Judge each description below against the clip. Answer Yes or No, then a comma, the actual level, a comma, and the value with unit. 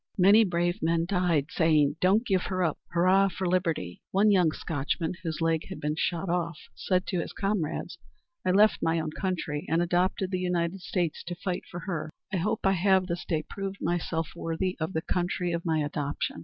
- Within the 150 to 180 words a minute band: No, average, 195 wpm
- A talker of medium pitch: Yes, medium, 175 Hz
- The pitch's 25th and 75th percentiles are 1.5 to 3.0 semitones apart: Yes, narrow, 2.5 semitones